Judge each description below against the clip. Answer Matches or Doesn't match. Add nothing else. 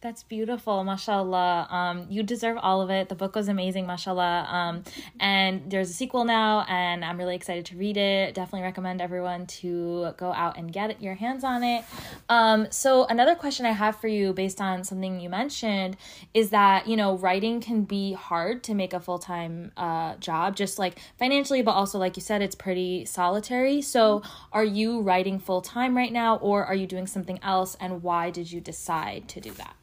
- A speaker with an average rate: Matches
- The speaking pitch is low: Doesn't match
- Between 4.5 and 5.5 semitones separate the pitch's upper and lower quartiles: Doesn't match